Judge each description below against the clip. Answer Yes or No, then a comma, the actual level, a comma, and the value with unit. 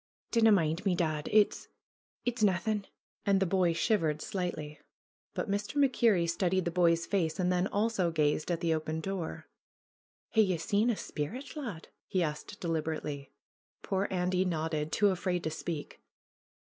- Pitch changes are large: No, average, 3.9 semitones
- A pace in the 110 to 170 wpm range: Yes, average, 160 wpm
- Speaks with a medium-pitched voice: Yes, medium, 180 Hz